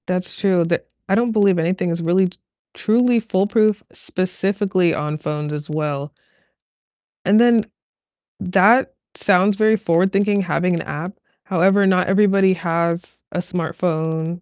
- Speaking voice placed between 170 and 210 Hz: Yes, medium, 185 Hz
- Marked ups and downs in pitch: No, average, 3.3 semitones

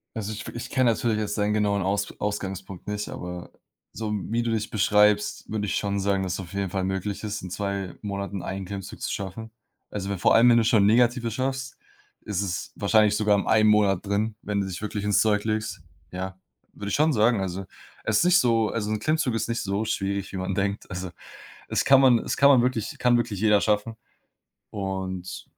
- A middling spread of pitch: No, narrow, 2.3 semitones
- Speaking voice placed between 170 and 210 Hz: No, low, 105 Hz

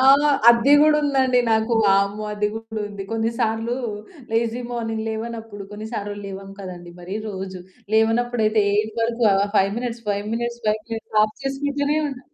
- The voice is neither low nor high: No, high, 225 Hz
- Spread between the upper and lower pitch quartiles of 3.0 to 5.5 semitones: No, narrow, 2.5 semitones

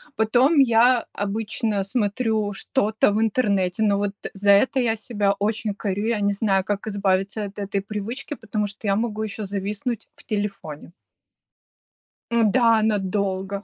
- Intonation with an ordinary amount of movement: No, narrow, 2.0 semitones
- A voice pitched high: Yes, high, 210 Hz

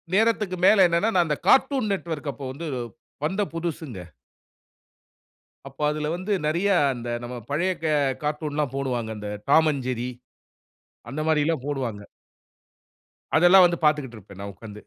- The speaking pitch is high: No, medium, 150 Hz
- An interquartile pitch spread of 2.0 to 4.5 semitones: No, average, 5.1 semitones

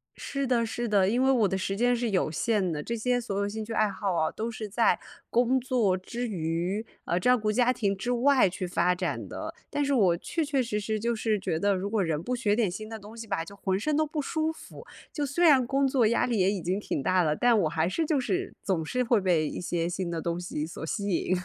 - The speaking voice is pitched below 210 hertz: No, high, 215 Hz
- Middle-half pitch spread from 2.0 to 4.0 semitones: No, average, 4.9 semitones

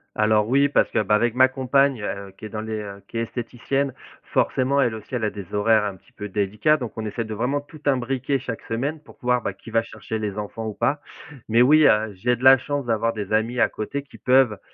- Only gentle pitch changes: No, average, 3.6 semitones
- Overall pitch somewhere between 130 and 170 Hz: No, low, 115 Hz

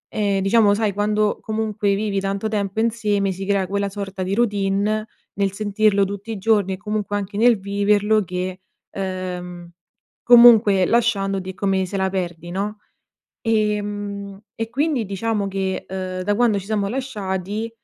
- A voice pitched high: Yes, high, 200 Hz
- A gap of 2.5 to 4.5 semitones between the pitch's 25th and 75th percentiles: No, narrow, 1.9 semitones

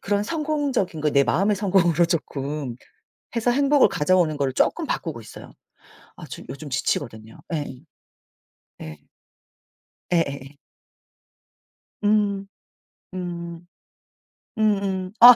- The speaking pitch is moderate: Yes, medium, 175 Hz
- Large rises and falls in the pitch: Yes, wide, 6.0 semitones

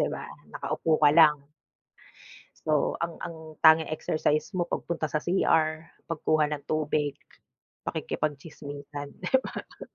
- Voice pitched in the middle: Yes, medium, 155 Hz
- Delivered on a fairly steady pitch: Yes, narrow, 1.4 semitones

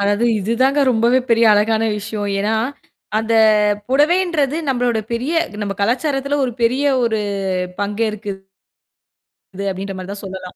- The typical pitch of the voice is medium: No, high, 225 Hz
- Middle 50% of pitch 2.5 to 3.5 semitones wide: No, average, 3.9 semitones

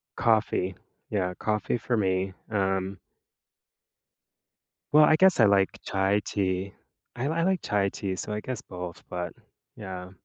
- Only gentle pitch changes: No, average, 3.1 semitones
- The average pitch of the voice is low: Yes, low, 100 Hz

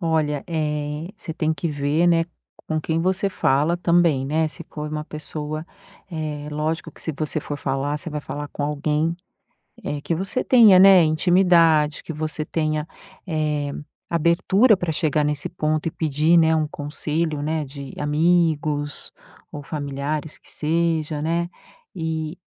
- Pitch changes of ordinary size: No, narrow, 2.0 semitones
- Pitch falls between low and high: Yes, medium, 155 Hz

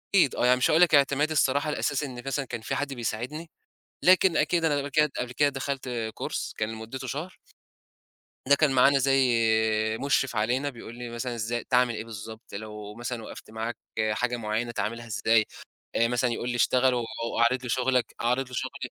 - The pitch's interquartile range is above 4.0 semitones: No, average, 3.2 semitones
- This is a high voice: No, low, 125 Hz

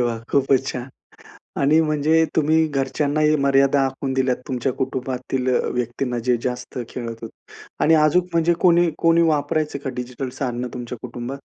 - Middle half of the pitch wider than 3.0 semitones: Yes, average, 3.5 semitones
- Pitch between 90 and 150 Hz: Yes, low, 135 Hz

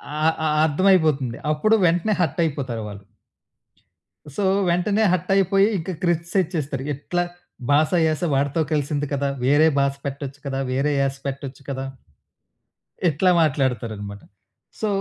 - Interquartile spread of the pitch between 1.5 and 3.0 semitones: No, average, 4.2 semitones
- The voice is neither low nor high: Yes, medium, 145 Hz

